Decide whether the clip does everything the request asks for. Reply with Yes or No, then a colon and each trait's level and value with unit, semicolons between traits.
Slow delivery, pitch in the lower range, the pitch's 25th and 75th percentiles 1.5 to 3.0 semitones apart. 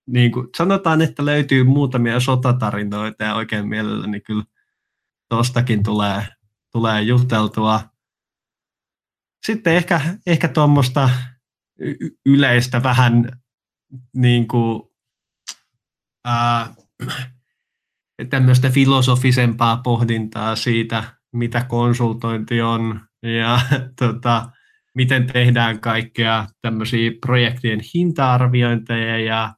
Yes: slow, 80 wpm; low, 120 Hz; narrow, 2.4 semitones